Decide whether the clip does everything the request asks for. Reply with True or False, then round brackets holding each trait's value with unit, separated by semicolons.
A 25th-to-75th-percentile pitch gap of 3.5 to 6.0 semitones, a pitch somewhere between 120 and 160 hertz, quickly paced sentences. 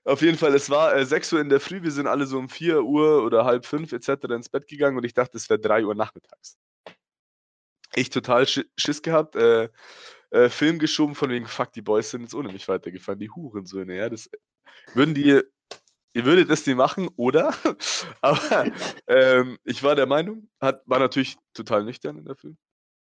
True (3.9 semitones; 140 Hz; 205 wpm)